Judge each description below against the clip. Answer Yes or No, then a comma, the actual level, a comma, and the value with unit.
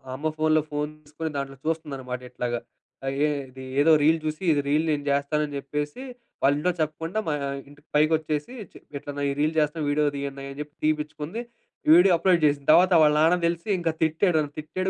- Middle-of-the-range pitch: Yes, medium, 150 Hz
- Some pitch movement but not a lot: No, narrow, 2.1 semitones